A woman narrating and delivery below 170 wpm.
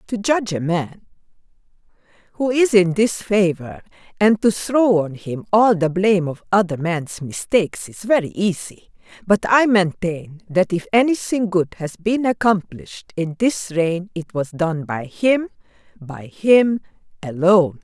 Yes: female; average, 150 wpm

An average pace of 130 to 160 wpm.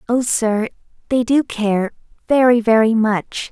Yes: slow, 135 wpm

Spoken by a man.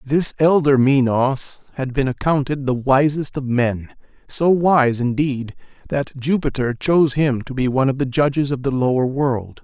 Yes: male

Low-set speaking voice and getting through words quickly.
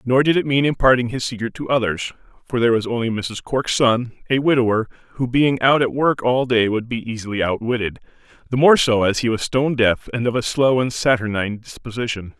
Yes: low, 120 Hz; fast, 215 wpm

